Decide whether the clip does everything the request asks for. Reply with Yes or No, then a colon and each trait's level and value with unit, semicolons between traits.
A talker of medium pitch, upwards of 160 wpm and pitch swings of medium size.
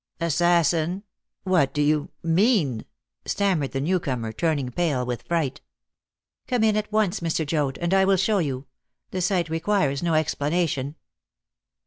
No: medium, 165 Hz; average, 145 wpm; average, 4.6 semitones